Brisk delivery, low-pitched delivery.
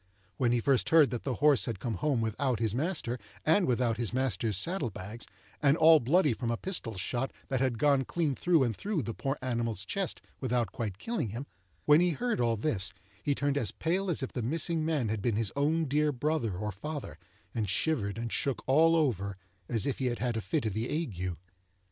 Yes: fast, 215 wpm; low, 130 Hz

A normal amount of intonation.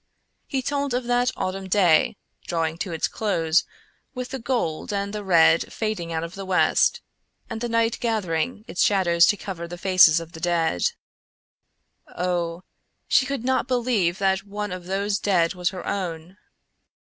Yes: average, 4.6 semitones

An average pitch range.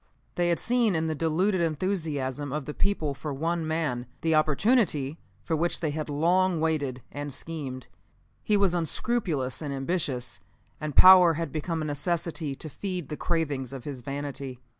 Yes: average, 3.6 semitones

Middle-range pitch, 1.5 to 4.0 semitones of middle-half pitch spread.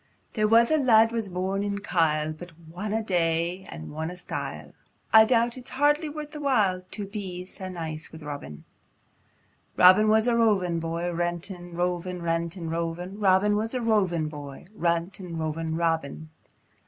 No: medium, 180 Hz; average, 4.4 semitones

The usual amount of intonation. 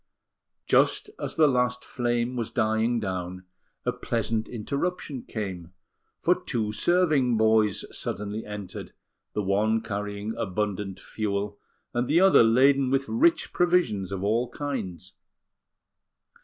Yes: average, 4.0 semitones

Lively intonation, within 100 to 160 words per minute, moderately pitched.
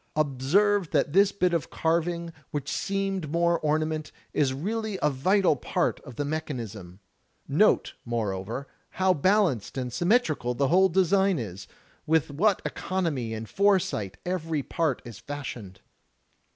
Yes: wide, 6.2 semitones; average, 140 wpm; medium, 155 Hz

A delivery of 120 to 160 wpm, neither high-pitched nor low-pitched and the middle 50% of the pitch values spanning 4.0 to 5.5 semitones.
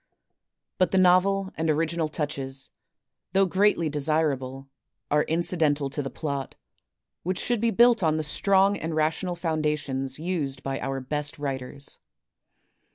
Yes: average, 140 wpm; medium, 155 Hz; average, 4.4 semitones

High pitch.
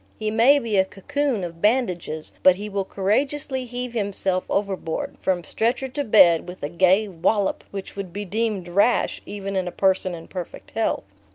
Yes: high, 200 Hz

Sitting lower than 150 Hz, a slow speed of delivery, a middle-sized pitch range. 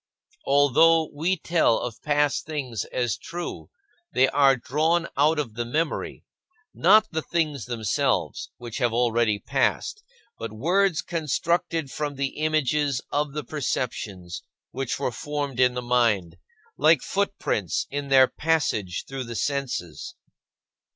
Yes: medium, 140 Hz; slow, 130 wpm; average, 4.6 semitones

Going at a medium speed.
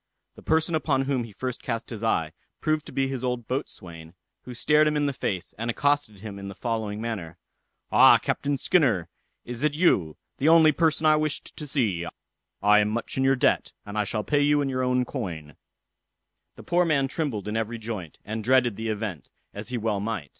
No: fast, 210 wpm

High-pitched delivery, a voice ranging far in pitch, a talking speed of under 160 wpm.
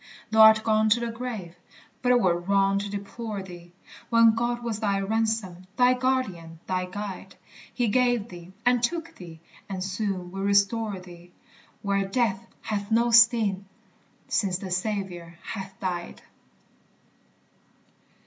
No: high, 200 Hz; average, 3.6 semitones; average, 140 wpm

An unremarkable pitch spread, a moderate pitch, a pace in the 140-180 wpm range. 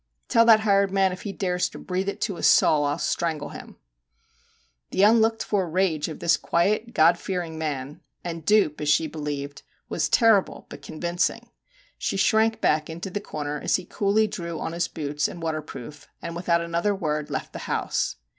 No: average, 4.4 semitones; medium, 170 Hz; average, 190 wpm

